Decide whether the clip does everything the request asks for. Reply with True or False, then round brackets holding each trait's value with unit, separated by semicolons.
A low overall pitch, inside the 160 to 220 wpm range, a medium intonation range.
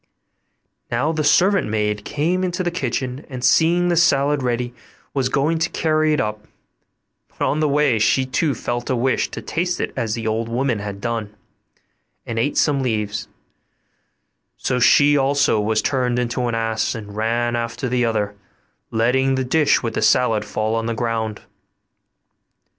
True (125 Hz; 170 wpm; 4.3 semitones)